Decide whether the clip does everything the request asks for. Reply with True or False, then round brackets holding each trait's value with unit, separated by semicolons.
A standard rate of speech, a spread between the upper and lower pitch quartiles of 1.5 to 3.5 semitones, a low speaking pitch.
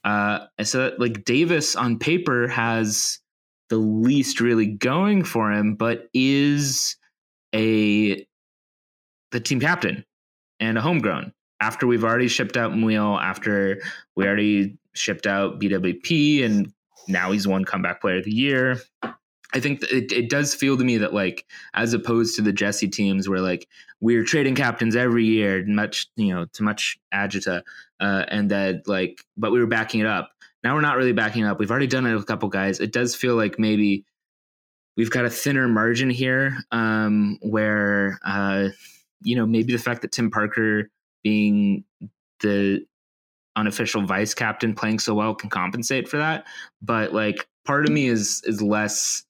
True (170 wpm; 3.0 semitones; 110 Hz)